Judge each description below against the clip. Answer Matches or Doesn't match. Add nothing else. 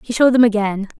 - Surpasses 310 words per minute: Doesn't match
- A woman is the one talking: Matches